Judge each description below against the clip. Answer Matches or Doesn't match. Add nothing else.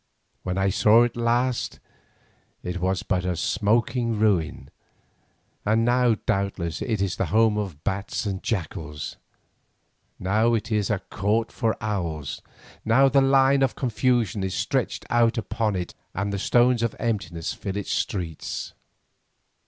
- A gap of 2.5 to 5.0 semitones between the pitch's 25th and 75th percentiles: Matches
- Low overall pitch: Matches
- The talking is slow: Doesn't match